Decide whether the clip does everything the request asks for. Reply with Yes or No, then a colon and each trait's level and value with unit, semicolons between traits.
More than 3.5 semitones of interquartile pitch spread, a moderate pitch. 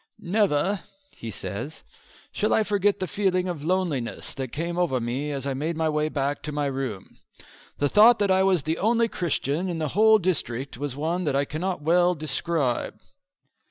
Yes: average, 4.9 semitones; medium, 160 Hz